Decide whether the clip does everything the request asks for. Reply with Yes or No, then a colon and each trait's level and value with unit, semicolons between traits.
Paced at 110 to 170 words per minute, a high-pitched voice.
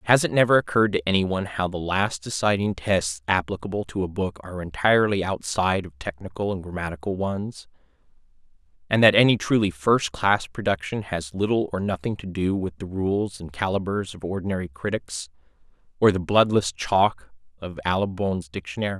No: average, 160 wpm; very low, 95 Hz